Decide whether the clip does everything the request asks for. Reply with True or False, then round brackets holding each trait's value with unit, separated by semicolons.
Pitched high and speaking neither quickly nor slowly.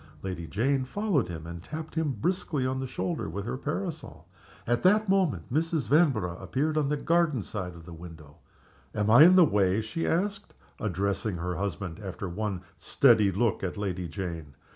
False (110 Hz; 180 wpm)